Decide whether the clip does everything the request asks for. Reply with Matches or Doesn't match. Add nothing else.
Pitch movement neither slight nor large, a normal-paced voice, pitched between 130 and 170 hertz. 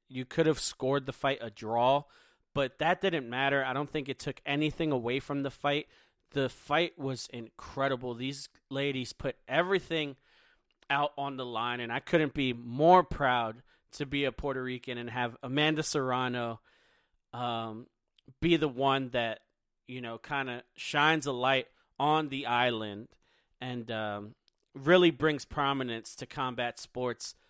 Matches